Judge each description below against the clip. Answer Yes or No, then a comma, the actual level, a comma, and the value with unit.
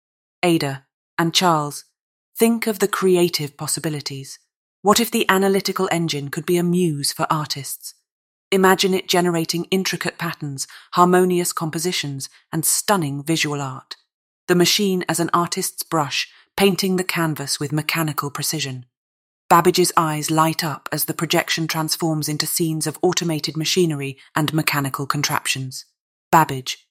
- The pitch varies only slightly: No, average, 3.4 semitones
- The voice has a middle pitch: Yes, medium, 160 Hz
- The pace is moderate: No, slow, 130 wpm